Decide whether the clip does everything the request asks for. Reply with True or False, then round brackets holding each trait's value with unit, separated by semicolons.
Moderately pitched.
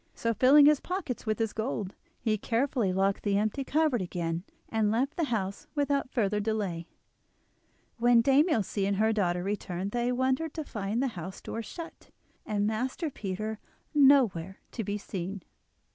False (220 Hz)